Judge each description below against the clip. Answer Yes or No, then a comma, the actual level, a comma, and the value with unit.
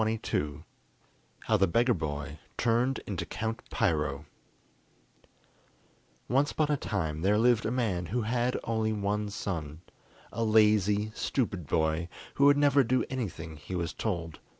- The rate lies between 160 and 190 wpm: No, average, 140 wpm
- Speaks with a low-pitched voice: Yes, low, 105 Hz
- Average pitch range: No, wide, 5.9 semitones